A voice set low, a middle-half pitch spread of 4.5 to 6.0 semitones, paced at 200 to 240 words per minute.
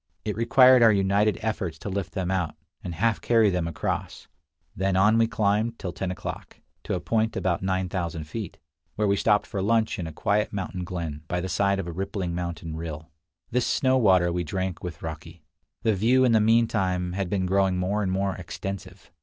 No: very low, 95 Hz; average, 3.3 semitones; fast, 205 wpm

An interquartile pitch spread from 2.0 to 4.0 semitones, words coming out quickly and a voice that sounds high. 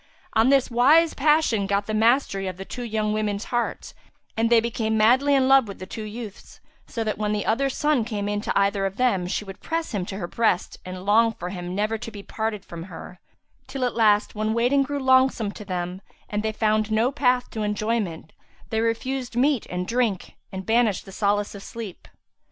Yes: average, 3.4 semitones; fast, 210 wpm; high, 220 Hz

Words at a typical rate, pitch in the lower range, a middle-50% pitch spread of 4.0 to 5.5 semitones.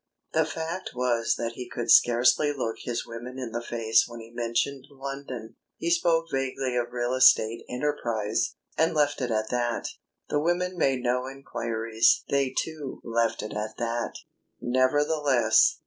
No: average, 155 wpm; low, 125 Hz; average, 3.2 semitones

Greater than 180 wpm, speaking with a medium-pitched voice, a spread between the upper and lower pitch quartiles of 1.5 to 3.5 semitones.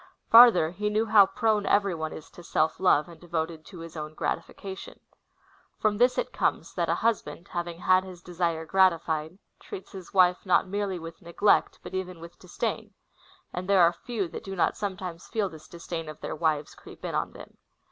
Yes: average, 200 wpm; medium, 180 Hz; average, 3.1 semitones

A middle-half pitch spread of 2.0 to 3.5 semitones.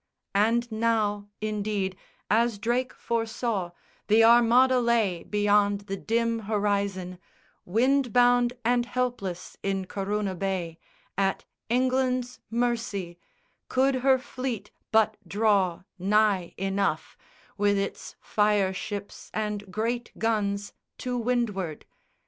Yes: average, 3.2 semitones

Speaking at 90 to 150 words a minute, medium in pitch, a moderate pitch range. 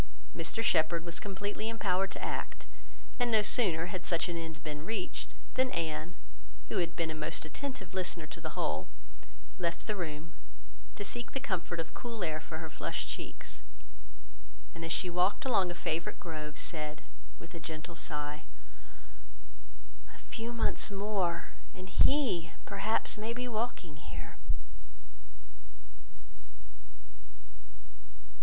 Yes: average, 140 wpm; medium, 175 Hz; average, 4.5 semitones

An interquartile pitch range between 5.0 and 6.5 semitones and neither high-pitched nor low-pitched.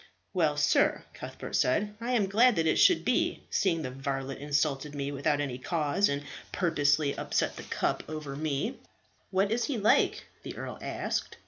Yes: wide, 5.6 semitones; medium, 155 Hz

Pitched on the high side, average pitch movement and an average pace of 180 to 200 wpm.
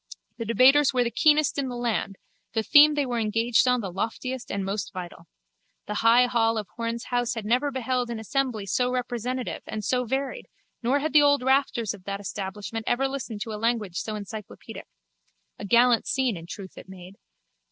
Yes: high, 235 Hz; average, 3.4 semitones; average, 195 wpm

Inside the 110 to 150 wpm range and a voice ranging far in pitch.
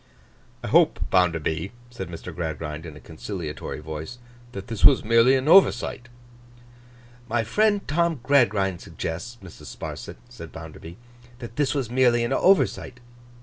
Yes: average, 140 wpm; wide, 7.8 semitones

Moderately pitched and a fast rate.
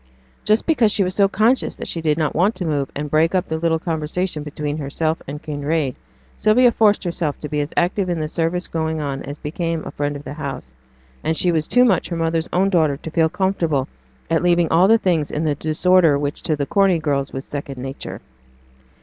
Yes: medium, 160 Hz; fast, 220 wpm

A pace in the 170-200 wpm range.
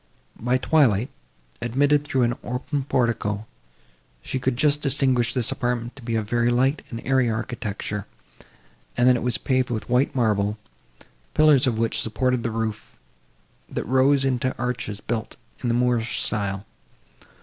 No: average, 155 wpm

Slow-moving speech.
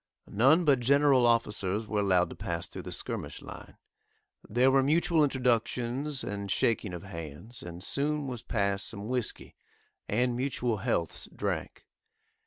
No: average, 145 wpm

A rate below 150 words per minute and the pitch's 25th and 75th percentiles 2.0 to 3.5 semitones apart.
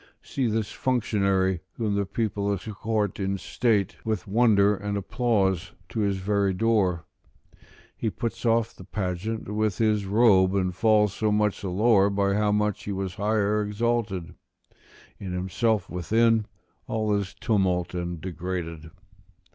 Yes: average, 140 wpm; narrow, 2.5 semitones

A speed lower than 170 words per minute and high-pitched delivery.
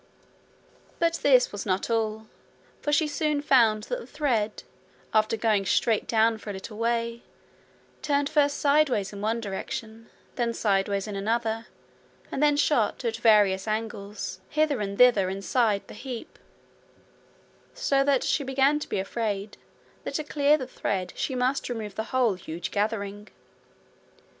Yes: average, 150 wpm; high, 225 Hz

